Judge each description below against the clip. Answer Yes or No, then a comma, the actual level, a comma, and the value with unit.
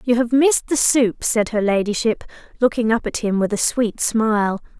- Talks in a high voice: Yes, high, 225 Hz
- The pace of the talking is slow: No, average, 200 wpm